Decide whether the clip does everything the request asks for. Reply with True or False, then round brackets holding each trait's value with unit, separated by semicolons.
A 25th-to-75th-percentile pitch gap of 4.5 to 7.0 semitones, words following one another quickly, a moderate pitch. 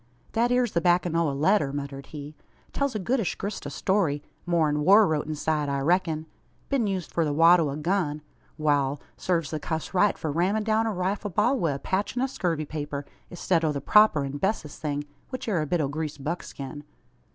True (5.0 semitones; 210 wpm; 165 Hz)